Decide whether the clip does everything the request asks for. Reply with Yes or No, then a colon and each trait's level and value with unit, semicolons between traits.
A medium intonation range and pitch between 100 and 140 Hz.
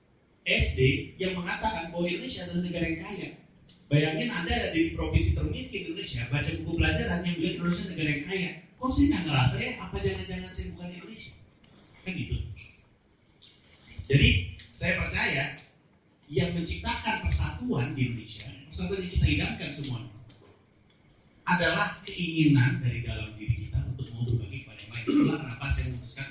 No: wide, 7.7 semitones; low, 135 Hz